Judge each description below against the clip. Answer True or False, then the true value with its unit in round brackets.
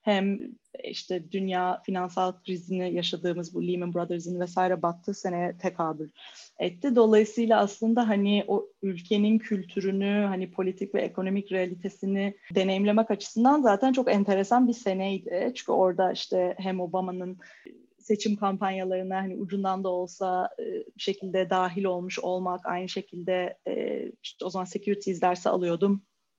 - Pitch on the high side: True (195 Hz)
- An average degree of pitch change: False (2.1 semitones)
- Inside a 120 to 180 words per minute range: True (125 wpm)